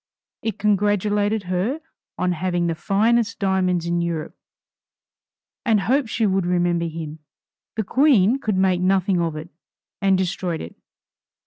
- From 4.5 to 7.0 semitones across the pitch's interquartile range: No, average, 3.4 semitones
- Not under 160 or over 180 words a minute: No, slow, 135 wpm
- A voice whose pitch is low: No, high, 190 Hz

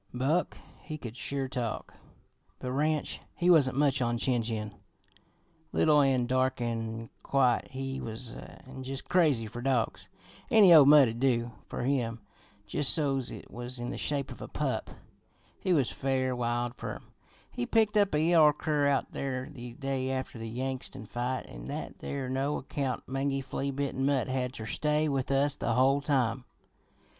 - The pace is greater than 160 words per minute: Yes, average, 170 wpm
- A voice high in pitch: No, low, 130 Hz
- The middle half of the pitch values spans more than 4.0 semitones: No, average, 2.7 semitones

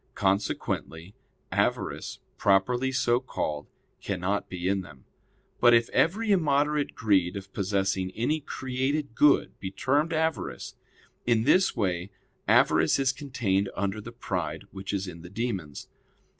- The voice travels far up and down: Yes, wide, 5.9 semitones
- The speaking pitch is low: Yes, low, 110 Hz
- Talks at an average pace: No, slow, 130 wpm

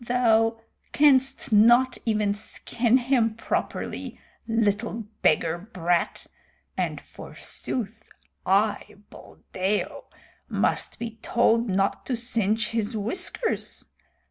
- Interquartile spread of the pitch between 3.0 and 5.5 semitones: No, narrow, 2.5 semitones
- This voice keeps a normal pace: No, slow, 90 wpm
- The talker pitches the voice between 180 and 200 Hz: No, high, 225 Hz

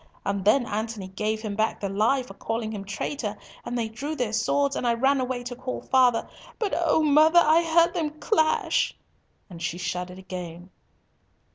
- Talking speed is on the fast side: No, average, 180 wpm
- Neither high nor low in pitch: No, high, 235 Hz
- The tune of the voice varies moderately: No, wide, 5.8 semitones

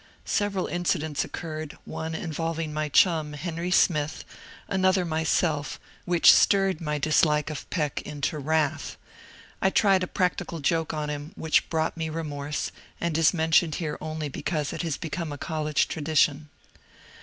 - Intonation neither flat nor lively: No, narrow, 2.1 semitones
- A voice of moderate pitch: Yes, medium, 160 Hz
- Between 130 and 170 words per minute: Yes, average, 155 wpm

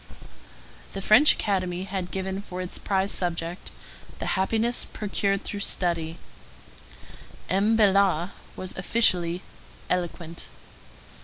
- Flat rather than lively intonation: Yes, narrow, 2.1 semitones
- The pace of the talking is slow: Yes, slow, 100 wpm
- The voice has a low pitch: No, high, 190 Hz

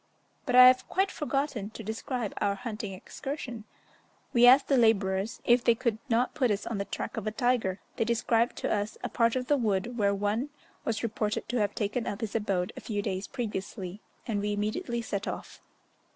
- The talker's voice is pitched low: No, high, 225 Hz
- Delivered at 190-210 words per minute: Yes, average, 200 wpm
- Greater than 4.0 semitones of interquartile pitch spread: No, average, 3.2 semitones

